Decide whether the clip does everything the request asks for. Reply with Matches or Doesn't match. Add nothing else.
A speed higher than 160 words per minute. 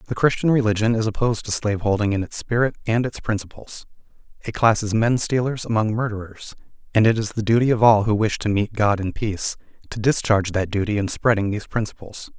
Matches